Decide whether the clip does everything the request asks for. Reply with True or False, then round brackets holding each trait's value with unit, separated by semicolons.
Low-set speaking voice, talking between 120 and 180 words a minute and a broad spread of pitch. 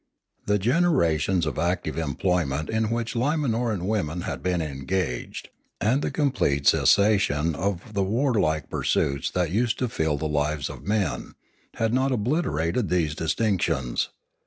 True (95 Hz; 150 wpm; 6.6 semitones)